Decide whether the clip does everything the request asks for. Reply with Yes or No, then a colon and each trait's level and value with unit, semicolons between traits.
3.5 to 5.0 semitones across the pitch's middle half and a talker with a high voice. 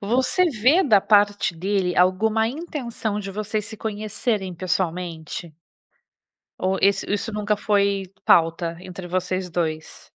No: average, 3.0 semitones; high, 200 Hz